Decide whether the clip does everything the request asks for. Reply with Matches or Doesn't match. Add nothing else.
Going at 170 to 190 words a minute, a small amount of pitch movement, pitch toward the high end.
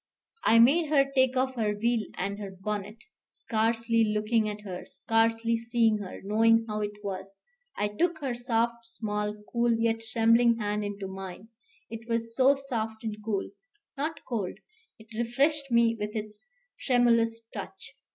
Doesn't match